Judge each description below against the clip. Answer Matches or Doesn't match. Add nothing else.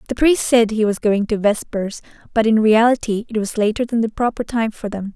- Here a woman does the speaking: Matches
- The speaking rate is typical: Doesn't match